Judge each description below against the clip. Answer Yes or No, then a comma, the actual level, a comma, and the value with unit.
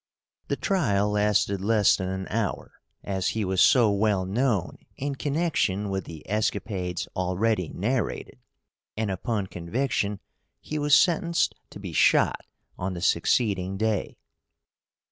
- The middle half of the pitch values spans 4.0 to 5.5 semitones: No, average, 3.6 semitones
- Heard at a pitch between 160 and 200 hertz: No, low, 105 Hz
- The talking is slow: Yes, slow, 130 wpm